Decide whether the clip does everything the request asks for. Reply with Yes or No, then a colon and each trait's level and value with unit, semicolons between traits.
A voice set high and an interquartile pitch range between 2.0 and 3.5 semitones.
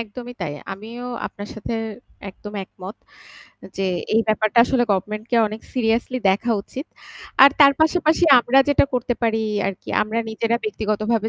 Yes: high, 225 Hz; narrow, 2.6 semitones